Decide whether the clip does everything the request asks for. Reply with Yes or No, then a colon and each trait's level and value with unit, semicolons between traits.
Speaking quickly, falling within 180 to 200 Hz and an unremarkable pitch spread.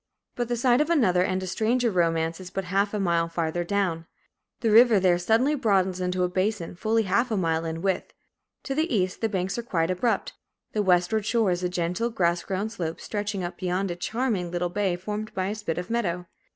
Yes: fast, 215 wpm; high, 190 Hz; average, 3.8 semitones